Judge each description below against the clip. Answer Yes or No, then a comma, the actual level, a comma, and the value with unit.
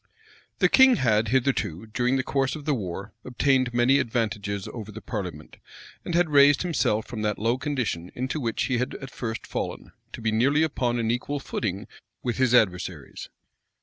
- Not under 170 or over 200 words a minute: Yes, average, 180 wpm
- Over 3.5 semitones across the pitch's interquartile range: Yes, average, 4.0 semitones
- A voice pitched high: No, low, 120 Hz